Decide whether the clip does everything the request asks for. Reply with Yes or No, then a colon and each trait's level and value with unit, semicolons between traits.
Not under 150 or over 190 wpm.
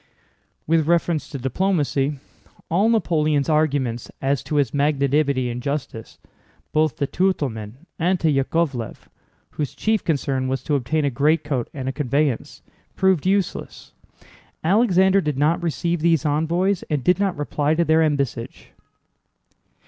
No: slow, 135 wpm